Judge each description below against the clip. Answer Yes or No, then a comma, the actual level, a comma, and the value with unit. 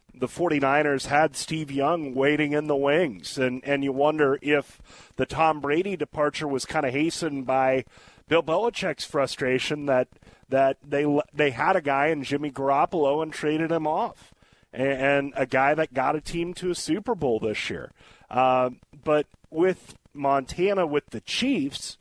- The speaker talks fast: No, average, 165 wpm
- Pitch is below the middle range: No, medium, 145 Hz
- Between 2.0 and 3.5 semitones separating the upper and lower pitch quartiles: Yes, average, 2.7 semitones